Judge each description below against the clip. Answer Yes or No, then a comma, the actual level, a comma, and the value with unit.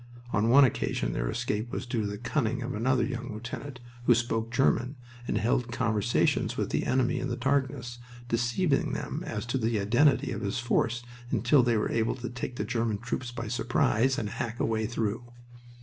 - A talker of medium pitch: No, low, 120 Hz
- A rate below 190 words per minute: No, average, 195 wpm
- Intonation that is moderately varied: No, narrow, 2.2 semitones